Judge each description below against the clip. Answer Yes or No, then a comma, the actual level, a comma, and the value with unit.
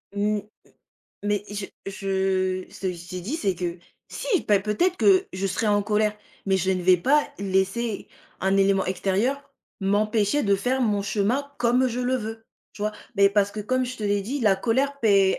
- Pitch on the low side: No, high, 205 Hz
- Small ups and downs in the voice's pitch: No, average, 3.7 semitones